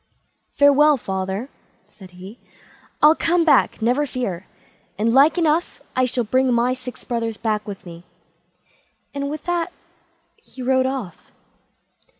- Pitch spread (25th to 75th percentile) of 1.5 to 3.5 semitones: No, average, 5.1 semitones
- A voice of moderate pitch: No, very high, 255 Hz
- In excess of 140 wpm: No, slow, 135 wpm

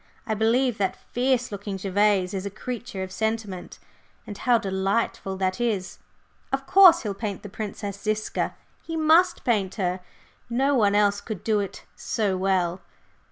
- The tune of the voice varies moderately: Yes, average, 3.6 semitones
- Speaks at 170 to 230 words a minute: No, average, 160 wpm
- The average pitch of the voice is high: Yes, high, 205 Hz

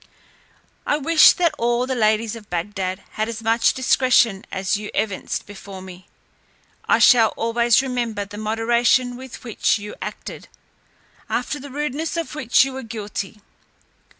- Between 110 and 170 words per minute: Yes, average, 150 wpm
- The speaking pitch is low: No, high, 230 Hz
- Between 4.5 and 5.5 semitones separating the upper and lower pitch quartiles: No, average, 3.7 semitones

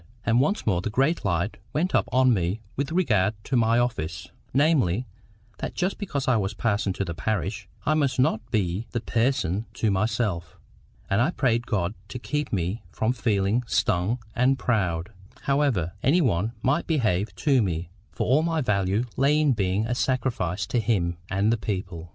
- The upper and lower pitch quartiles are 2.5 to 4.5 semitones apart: No, wide, 5.5 semitones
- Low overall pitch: Yes, low, 110 Hz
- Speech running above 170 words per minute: Yes, average, 180 wpm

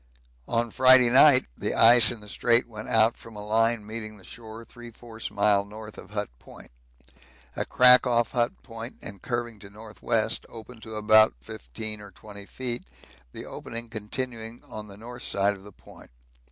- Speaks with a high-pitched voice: No, low, 110 Hz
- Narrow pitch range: Yes, narrow, 2.0 semitones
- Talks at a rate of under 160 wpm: No, average, 175 wpm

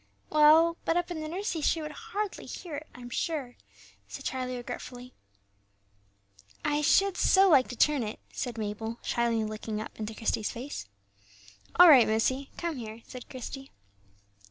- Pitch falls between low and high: No, very high, 265 Hz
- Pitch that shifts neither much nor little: No, wide, 5.8 semitones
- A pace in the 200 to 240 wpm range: No, average, 155 wpm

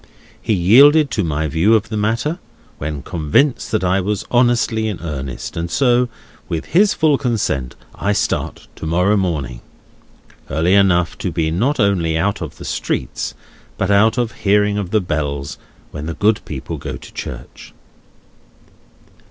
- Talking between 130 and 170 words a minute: Yes, average, 160 wpm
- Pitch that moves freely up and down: Yes, wide, 5.8 semitones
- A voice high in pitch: No, very low, 95 Hz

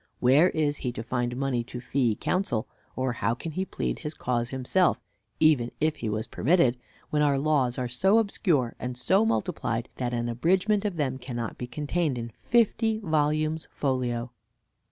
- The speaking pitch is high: No, low, 135 Hz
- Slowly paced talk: No, average, 175 wpm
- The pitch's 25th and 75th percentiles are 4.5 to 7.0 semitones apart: Yes, average, 5.1 semitones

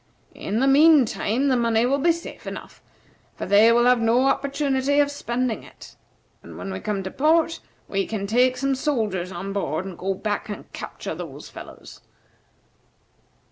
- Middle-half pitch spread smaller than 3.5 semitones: No, average, 5.2 semitones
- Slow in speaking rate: No, average, 175 wpm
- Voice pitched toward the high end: Yes, high, 240 Hz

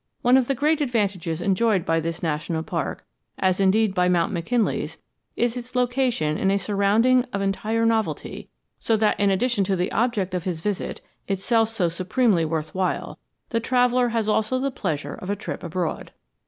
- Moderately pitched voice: No, high, 205 Hz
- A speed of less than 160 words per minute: No, average, 180 wpm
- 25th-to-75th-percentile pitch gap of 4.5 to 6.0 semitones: Yes, average, 4.8 semitones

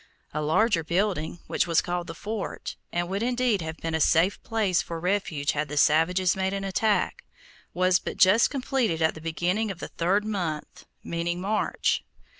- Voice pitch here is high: No, medium, 180 Hz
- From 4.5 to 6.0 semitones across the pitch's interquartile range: No, average, 3.8 semitones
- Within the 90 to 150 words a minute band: No, average, 180 wpm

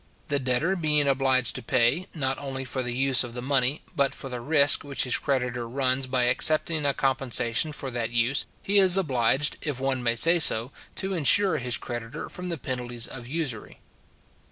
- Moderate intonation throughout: Yes, average, 3.1 semitones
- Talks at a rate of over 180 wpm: Yes, average, 190 wpm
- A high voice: No, low, 130 Hz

